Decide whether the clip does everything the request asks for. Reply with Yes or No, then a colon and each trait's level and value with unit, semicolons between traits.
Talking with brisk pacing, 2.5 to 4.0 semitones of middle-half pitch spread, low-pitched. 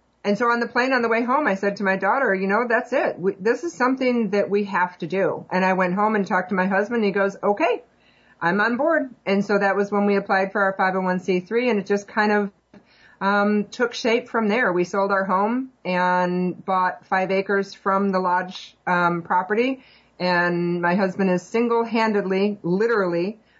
No: fast, 210 wpm; average, 3.5 semitones; high, 200 Hz